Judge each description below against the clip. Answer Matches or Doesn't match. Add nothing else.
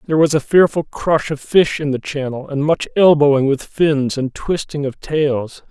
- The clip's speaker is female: Doesn't match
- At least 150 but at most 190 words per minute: Doesn't match